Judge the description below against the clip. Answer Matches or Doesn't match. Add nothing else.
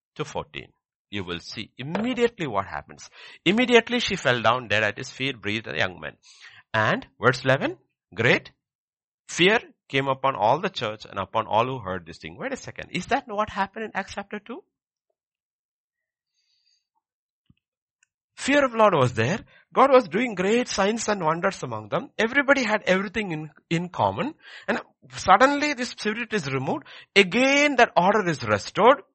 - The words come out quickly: Doesn't match